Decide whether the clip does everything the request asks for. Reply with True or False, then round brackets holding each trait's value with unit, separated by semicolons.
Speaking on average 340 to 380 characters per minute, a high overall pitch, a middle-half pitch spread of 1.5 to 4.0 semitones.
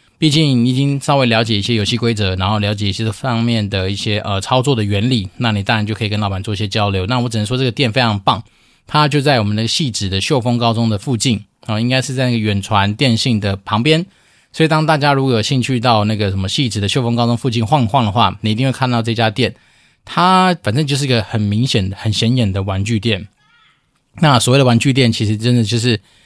False (355 characters per minute; 115 Hz; 3.6 semitones)